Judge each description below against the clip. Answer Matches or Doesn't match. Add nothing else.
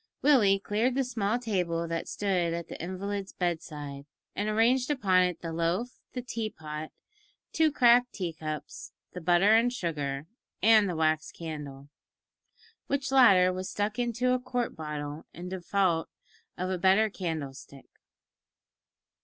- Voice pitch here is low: Doesn't match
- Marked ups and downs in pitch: Matches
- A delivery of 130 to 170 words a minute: Matches